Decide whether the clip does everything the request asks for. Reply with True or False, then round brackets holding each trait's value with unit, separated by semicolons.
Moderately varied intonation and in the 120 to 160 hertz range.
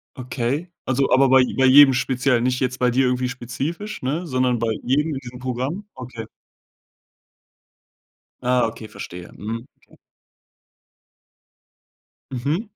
False (1.9 semitones; 130 Hz)